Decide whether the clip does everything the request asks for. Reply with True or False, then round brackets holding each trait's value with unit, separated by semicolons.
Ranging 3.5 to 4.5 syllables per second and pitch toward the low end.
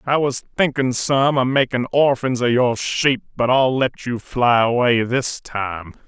True (4.0 syllables/s; 125 Hz)